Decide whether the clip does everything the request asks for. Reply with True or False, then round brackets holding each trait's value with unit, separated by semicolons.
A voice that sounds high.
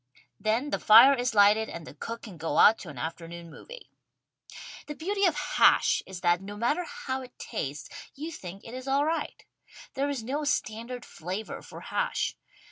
True (230 Hz)